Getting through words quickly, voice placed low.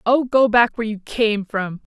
No: fast, 210 wpm; high, 225 Hz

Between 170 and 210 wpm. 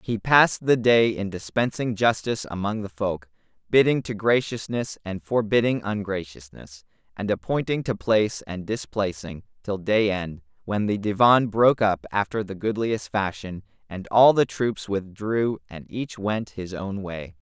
No: average, 155 wpm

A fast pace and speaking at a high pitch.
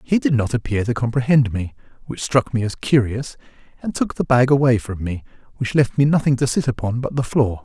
No: fast, 230 wpm; low, 125 Hz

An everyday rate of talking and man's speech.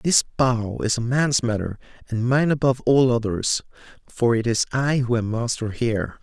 Yes: average, 185 wpm; male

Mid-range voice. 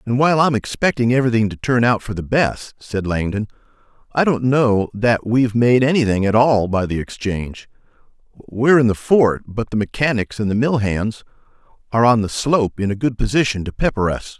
No: low, 115 Hz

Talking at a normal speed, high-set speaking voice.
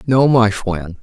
No: average, 175 wpm; low, 110 Hz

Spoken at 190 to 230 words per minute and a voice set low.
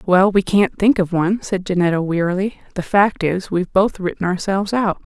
No: average, 200 wpm; high, 190 Hz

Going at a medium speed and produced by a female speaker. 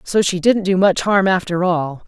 No: fast, 230 wpm; female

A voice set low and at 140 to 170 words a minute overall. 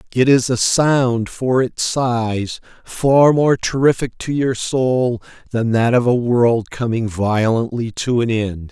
Yes: low, 120 Hz; average, 160 wpm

